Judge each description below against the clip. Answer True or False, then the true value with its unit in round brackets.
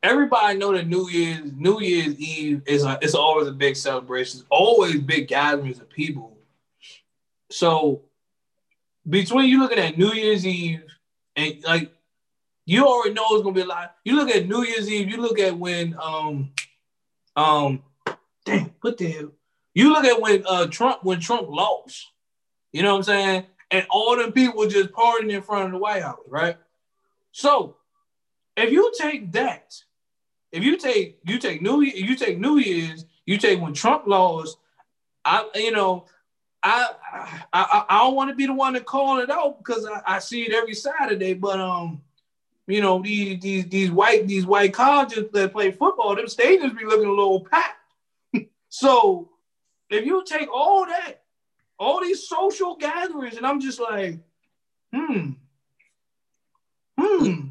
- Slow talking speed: False (170 wpm)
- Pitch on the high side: True (200 Hz)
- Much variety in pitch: True (7.8 semitones)